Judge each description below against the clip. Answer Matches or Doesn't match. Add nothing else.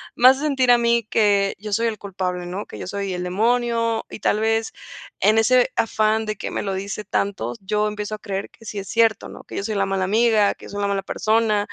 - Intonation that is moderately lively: Doesn't match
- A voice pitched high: Matches